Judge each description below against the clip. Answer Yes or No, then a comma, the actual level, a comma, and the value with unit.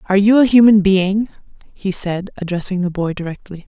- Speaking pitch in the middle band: No, high, 195 Hz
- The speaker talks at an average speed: Yes, average, 175 wpm